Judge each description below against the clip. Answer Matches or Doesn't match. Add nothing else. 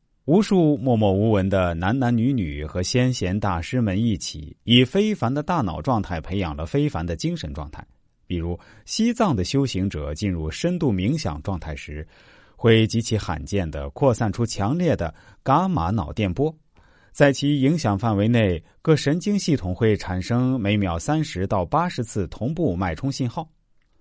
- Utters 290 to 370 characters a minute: Doesn't match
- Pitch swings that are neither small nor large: Doesn't match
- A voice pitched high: Doesn't match